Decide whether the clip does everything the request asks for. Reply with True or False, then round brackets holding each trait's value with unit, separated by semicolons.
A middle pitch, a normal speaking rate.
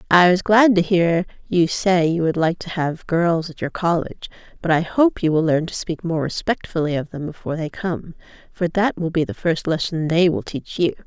False (170 Hz; 230 wpm)